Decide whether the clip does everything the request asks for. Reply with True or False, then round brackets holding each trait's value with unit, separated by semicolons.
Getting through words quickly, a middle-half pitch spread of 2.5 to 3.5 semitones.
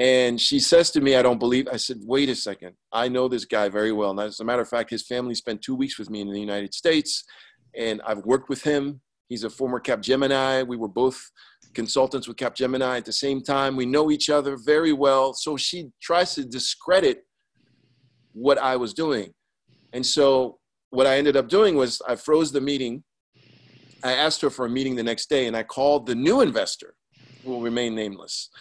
True (210 wpm; 2.9 semitones)